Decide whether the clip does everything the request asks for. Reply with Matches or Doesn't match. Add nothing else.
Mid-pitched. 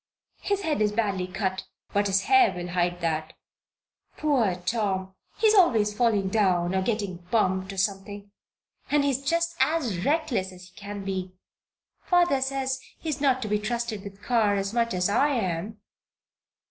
Doesn't match